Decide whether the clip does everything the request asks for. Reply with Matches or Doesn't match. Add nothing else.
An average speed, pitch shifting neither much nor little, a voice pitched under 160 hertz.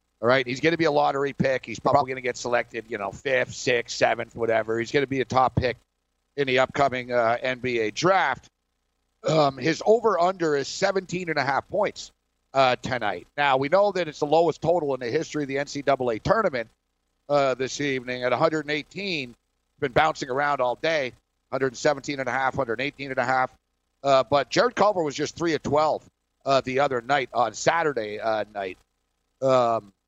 Matches